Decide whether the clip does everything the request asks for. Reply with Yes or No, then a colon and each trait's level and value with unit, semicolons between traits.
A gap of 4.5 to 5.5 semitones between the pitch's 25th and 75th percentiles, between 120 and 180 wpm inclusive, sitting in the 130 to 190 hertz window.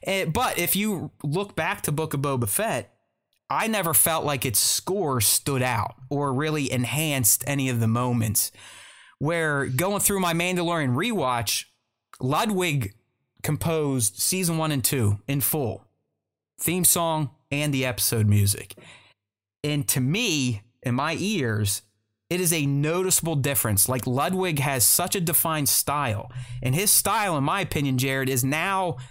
Yes: average, 4.8 semitones; average, 150 wpm; medium, 140 Hz